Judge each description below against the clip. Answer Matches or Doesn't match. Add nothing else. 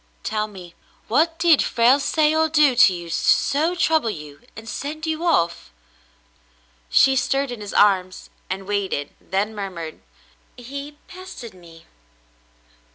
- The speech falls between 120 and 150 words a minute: Matches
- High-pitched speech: Matches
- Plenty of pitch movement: Matches